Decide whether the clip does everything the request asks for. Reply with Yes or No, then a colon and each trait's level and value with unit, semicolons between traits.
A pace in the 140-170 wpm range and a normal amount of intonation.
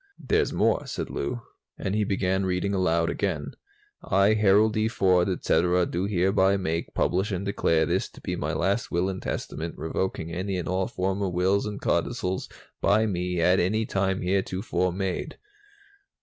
No: average, 165 wpm; narrow, 1.9 semitones